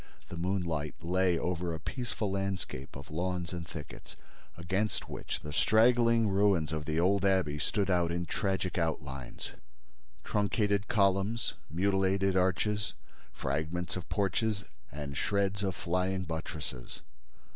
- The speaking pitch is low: Yes, very low, 90 Hz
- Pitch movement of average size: Yes, average, 3.4 semitones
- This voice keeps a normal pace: No, slow, 125 wpm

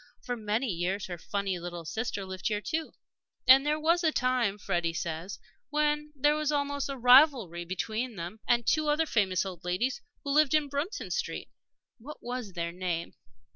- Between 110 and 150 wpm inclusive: No, average, 175 wpm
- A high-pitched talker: Yes, high, 235 Hz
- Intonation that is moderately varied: No, wide, 8.0 semitones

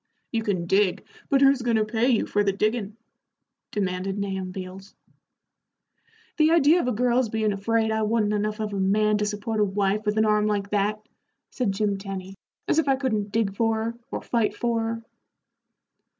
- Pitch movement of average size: No, narrow, 2.2 semitones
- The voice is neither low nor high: No, high, 215 Hz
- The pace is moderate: Yes, average, 190 wpm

